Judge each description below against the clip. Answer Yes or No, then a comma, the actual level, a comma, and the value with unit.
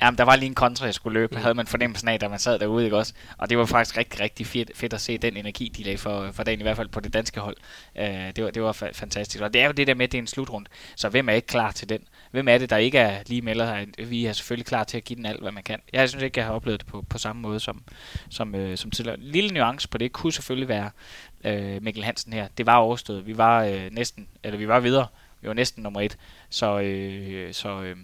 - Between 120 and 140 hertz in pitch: No, low, 110 Hz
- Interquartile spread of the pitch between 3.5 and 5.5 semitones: No, average, 2.7 semitones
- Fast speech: Yes, fast, 290 wpm